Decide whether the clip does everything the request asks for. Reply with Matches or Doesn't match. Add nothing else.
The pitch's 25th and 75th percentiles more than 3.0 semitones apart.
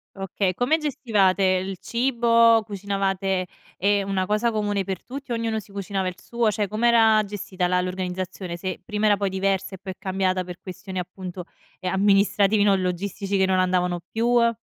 Doesn't match